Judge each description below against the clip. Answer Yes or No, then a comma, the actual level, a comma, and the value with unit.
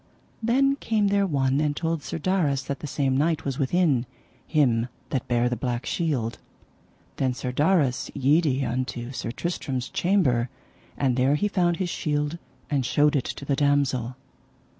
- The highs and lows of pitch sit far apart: No, average, 4.5 semitones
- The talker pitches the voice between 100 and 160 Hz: Yes, medium, 140 Hz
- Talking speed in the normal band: Yes, average, 160 wpm